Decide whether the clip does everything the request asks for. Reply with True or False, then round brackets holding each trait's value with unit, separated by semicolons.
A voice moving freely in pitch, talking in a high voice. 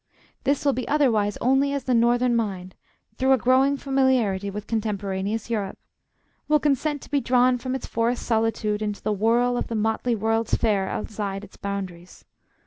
False (3.9 semitones; 230 Hz)